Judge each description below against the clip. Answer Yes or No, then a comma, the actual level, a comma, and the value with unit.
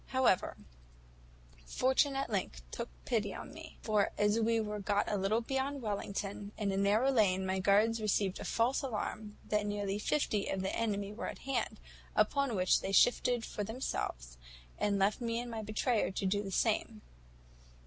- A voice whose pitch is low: No, high, 210 Hz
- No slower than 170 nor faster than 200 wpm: Yes, average, 175 wpm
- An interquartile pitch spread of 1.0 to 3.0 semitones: Yes, average, 2.7 semitones